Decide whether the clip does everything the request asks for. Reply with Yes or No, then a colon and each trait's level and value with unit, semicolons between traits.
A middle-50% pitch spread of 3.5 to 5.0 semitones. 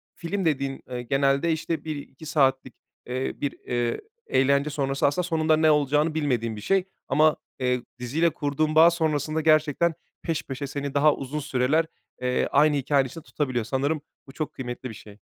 No: average, 2.9 semitones